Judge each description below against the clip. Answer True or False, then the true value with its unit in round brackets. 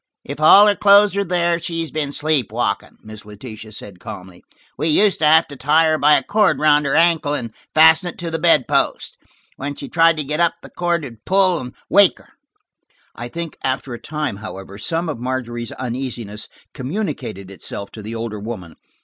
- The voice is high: False (145 Hz)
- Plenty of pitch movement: True (6.3 semitones)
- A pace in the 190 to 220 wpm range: True (195 wpm)